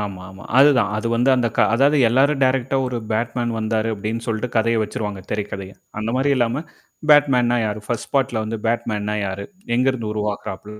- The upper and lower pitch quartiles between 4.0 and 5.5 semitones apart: No, average, 3.2 semitones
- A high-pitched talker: No, low, 115 Hz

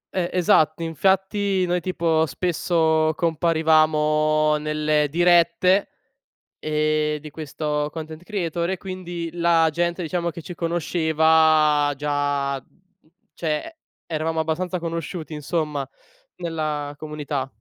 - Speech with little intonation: Yes, narrow, 2.2 semitones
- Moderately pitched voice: Yes, medium, 160 Hz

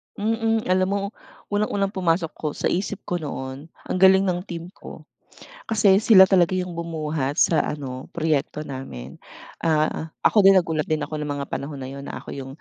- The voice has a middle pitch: Yes, medium, 165 Hz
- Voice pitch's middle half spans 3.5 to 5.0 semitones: Yes, average, 4.6 semitones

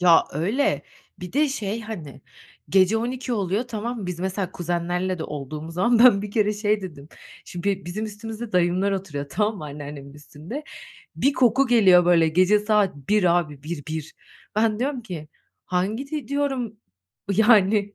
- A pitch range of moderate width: Yes, average, 4.5 semitones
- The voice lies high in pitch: Yes, high, 195 Hz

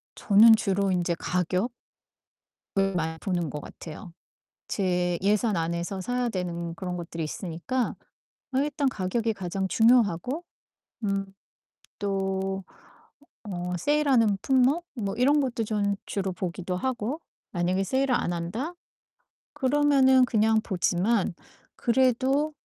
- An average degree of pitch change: No, wide, 5.7 semitones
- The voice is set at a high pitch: Yes, high, 200 Hz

